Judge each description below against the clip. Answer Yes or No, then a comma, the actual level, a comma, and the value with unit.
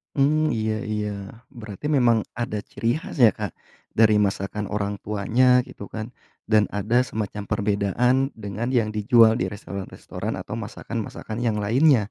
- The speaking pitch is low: Yes, low, 110 Hz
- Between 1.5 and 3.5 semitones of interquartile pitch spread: Yes, narrow, 2.4 semitones